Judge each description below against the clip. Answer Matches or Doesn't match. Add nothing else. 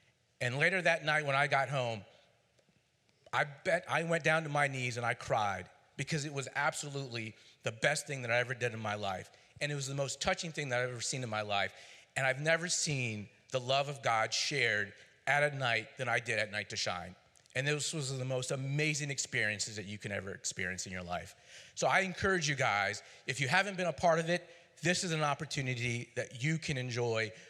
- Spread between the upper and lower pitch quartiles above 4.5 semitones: Matches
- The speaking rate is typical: Doesn't match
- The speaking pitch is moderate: Doesn't match